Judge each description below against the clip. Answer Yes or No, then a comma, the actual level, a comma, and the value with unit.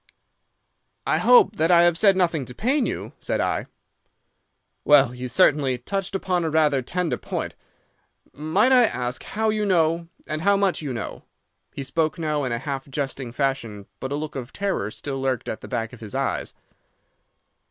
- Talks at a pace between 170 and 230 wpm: Yes, average, 180 wpm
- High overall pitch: No, medium, 150 Hz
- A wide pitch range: Yes, wide, 5.8 semitones